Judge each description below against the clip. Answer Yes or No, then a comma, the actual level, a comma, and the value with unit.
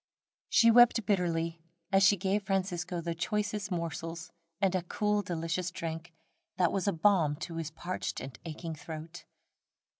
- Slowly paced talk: No, average, 150 wpm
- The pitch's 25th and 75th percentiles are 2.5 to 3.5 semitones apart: Yes, average, 3.1 semitones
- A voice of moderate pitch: Yes, medium, 175 Hz